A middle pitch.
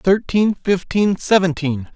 Yes: medium, 180 Hz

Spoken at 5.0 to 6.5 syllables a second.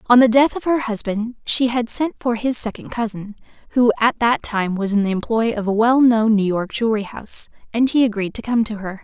Yes: 5.4 syllables/s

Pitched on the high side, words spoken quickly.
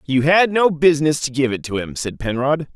No: medium, 155 Hz; fast, 240 wpm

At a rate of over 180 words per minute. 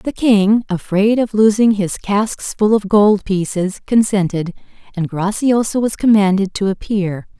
No: average, 145 wpm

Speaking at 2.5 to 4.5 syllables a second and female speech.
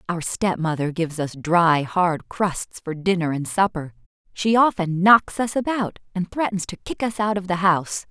No: 4.7 syllables/s; female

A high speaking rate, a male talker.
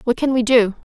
No: fast, 265 wpm; female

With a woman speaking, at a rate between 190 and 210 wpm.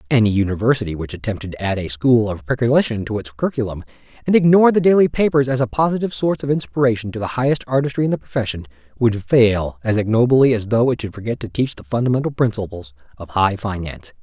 No: male; average, 200 wpm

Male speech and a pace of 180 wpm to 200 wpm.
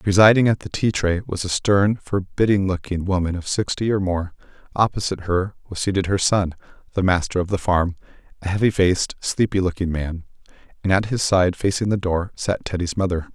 Yes: male; average, 190 wpm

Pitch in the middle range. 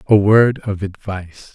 No: low, 100 Hz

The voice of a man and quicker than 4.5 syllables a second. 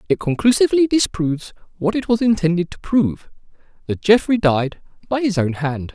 Yes: male; 5.6 syllables/s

